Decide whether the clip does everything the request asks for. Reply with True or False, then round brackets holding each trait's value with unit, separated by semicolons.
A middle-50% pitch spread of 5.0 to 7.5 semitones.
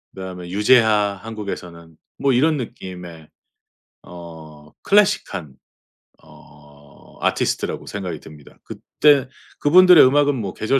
False (8.0 semitones)